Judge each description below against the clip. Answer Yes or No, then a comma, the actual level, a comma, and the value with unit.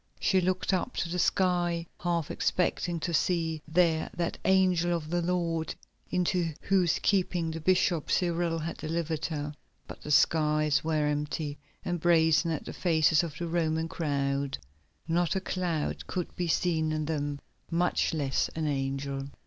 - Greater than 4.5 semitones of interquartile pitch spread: No, narrow, 2.4 semitones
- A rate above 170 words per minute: No, average, 155 wpm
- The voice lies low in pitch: No, medium, 165 Hz